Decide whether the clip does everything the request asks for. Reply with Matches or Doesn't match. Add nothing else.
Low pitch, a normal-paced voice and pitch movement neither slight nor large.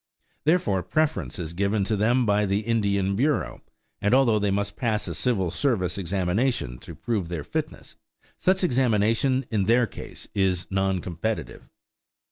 Matches